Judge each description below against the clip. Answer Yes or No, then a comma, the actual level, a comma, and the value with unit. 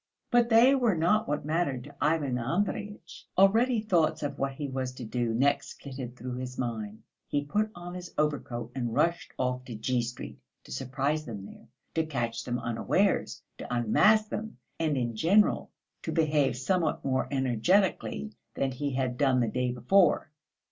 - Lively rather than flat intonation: Yes, wide, 5.7 semitones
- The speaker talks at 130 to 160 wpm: No, average, 170 wpm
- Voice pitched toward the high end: No, low, 135 Hz